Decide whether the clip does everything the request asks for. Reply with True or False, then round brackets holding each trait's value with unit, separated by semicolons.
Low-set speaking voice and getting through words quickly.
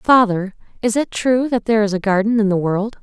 False (215 Hz; 240 wpm)